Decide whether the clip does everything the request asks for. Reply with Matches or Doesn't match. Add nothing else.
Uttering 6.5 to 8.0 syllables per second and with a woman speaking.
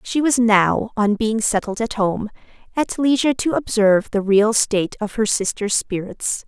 Doesn't match